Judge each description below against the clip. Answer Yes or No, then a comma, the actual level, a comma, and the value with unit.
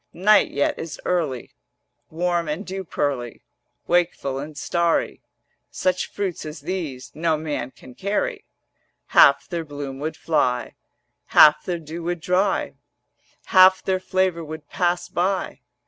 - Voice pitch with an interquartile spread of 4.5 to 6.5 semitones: No, average, 3.8 semitones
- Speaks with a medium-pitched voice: Yes, medium, 165 Hz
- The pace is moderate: No, slow, 130 wpm